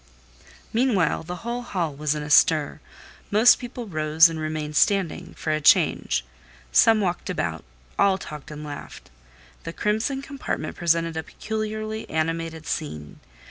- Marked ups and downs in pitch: Yes, wide, 6.0 semitones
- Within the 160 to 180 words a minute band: No, average, 140 wpm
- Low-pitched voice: No, medium, 165 Hz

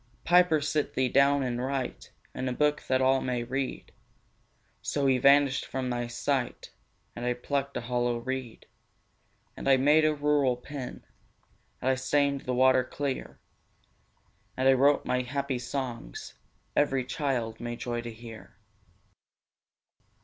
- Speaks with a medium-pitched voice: No, low, 130 Hz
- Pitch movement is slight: Yes, narrow, 2.3 semitones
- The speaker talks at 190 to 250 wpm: No, average, 145 wpm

